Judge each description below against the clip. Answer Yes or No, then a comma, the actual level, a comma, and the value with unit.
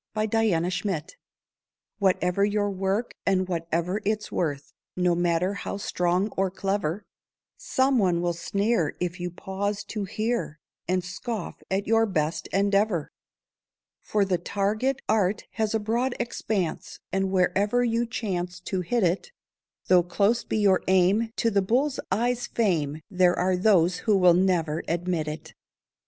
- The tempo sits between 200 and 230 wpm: No, average, 145 wpm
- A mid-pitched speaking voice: No, high, 195 Hz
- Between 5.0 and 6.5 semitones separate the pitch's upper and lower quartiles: No, average, 3.2 semitones